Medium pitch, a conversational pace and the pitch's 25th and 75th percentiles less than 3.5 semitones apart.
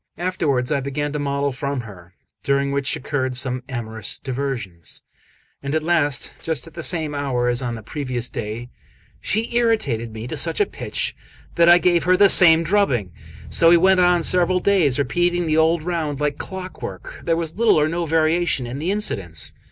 No: medium, 150 Hz; average, 185 wpm; wide, 5.4 semitones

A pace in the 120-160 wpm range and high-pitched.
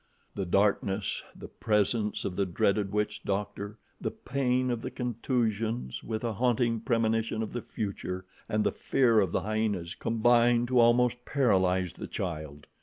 No: average, 155 wpm; low, 110 Hz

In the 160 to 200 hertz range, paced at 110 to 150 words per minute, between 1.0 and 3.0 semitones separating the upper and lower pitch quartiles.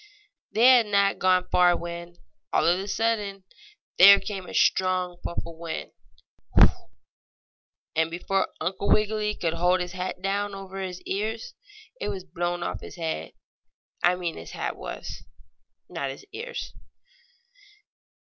Yes: medium, 185 Hz; average, 140 wpm; narrow, 2.5 semitones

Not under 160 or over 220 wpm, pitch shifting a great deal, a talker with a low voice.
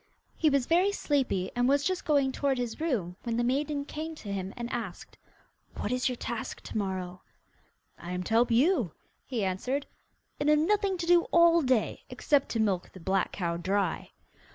No: average, 190 wpm; wide, 7.3 semitones; very high, 250 Hz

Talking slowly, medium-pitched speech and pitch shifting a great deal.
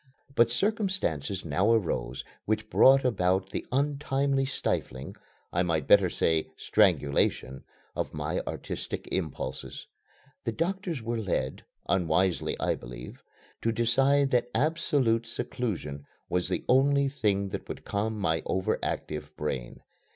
No: slow, 125 wpm; low, 110 Hz; wide, 8.7 semitones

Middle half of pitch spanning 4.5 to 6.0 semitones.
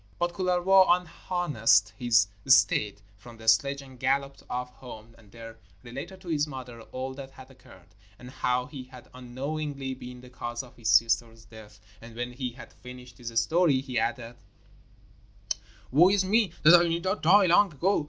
Yes: average, 4.9 semitones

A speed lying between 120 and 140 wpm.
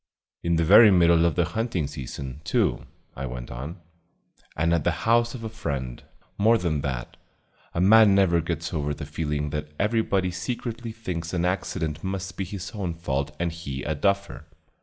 No: average, 180 wpm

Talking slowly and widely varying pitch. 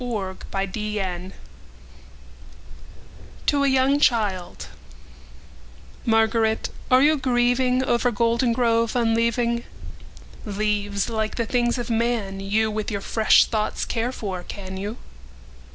No: slow, 95 wpm; average, 3.4 semitones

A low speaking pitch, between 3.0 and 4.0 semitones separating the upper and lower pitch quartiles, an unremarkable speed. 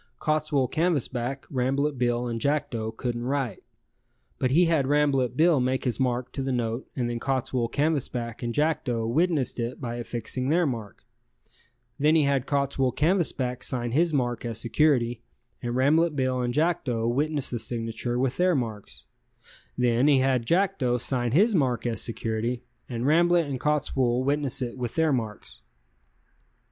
Yes: low, 130 Hz; average, 3.6 semitones; average, 155 wpm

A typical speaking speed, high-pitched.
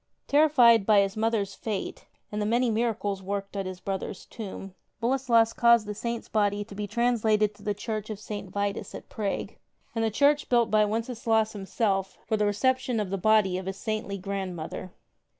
Yes: average, 180 wpm; high, 215 Hz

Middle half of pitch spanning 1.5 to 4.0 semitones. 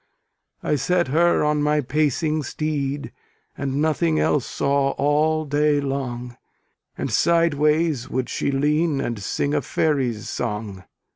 Yes: narrow, 2.4 semitones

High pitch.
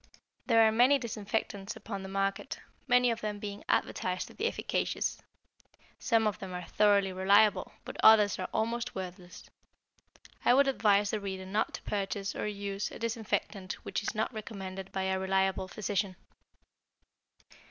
Yes: high, 205 Hz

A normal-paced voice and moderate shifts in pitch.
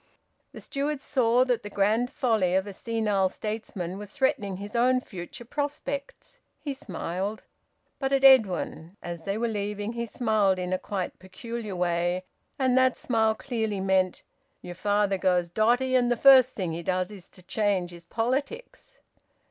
Yes: average, 165 wpm; average, 4.9 semitones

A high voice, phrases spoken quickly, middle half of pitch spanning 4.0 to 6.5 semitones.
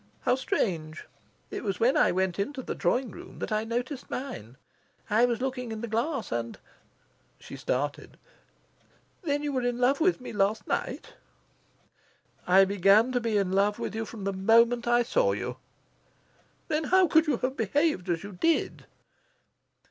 No: high, 230 Hz; average, 170 wpm; average, 5.1 semitones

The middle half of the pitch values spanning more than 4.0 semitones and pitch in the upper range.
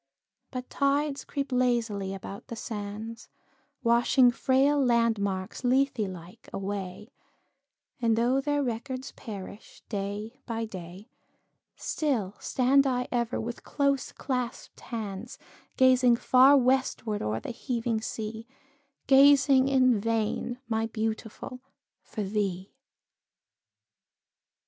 No: average, 3.7 semitones; high, 235 Hz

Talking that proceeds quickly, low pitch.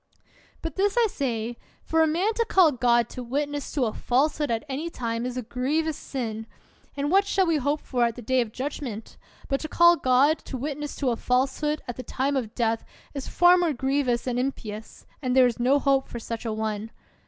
No: fast, 220 wpm; very high, 265 Hz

